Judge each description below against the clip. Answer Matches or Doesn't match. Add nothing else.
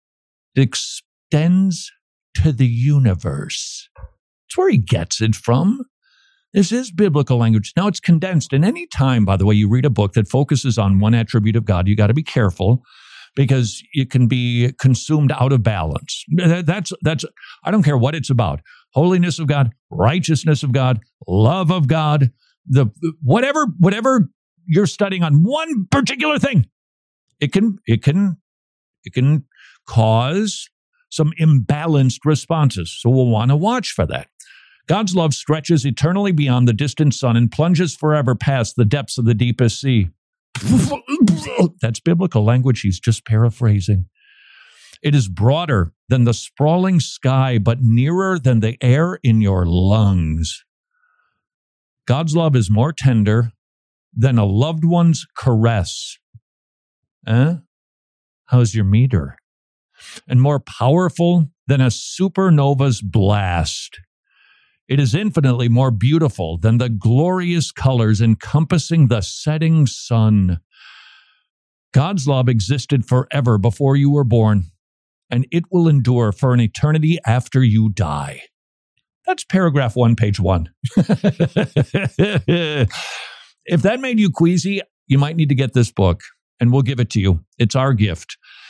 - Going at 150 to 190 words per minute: Doesn't match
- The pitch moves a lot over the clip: Matches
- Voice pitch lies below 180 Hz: Matches